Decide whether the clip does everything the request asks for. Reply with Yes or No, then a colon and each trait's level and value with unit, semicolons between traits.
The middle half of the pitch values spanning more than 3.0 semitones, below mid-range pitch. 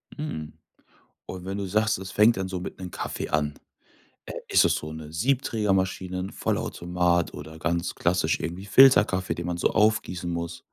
No: narrow, 2.4 semitones; very low, 90 Hz